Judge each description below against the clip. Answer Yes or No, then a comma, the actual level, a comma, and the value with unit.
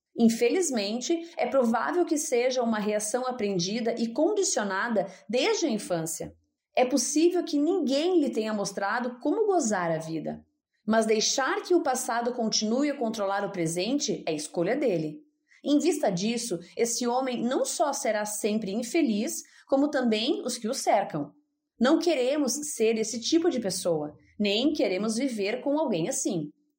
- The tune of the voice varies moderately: No, wide, 5.8 semitones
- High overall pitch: Yes, high, 240 Hz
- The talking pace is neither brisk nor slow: Yes, average, 150 wpm